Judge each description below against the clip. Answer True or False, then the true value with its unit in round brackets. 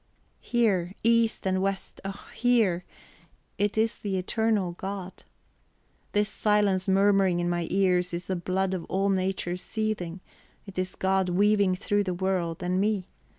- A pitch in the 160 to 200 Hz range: True (190 Hz)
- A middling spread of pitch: False (2.1 semitones)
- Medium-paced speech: True (150 wpm)